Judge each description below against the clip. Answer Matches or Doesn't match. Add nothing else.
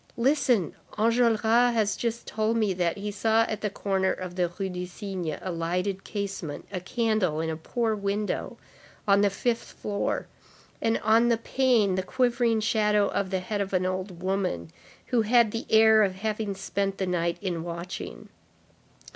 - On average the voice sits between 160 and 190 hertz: Doesn't match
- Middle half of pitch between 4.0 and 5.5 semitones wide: Doesn't match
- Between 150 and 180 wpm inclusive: Matches